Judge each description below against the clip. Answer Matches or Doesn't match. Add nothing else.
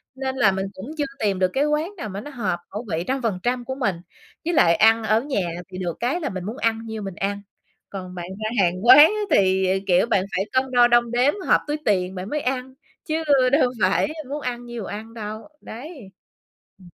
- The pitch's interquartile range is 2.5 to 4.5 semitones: Doesn't match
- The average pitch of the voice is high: Matches